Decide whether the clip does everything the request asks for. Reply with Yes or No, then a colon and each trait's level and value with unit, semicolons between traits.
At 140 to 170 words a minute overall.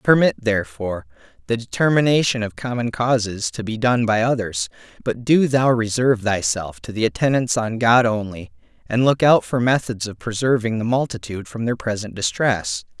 Yes: average, 165 wpm